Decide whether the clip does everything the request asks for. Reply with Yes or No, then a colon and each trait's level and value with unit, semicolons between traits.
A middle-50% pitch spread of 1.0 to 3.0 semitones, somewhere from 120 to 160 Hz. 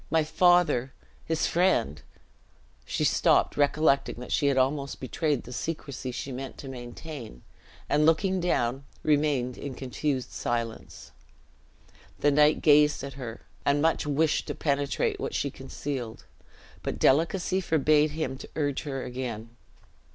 No: average, 3.4 semitones; medium, 140 Hz